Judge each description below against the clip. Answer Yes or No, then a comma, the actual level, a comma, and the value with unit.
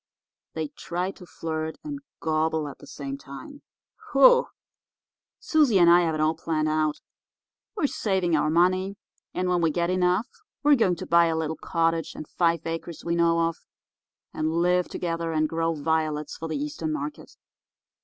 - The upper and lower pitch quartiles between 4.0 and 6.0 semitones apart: No, narrow, 2.4 semitones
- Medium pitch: Yes, medium, 165 Hz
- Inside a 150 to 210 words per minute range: Yes, average, 170 wpm